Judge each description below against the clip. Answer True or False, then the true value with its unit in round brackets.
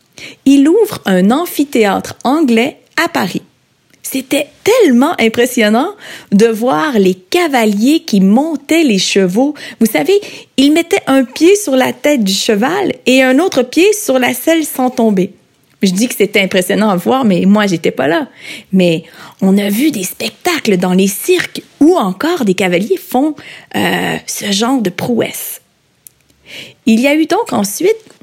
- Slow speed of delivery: False (160 wpm)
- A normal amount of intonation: False (7.0 semitones)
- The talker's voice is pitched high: True (245 Hz)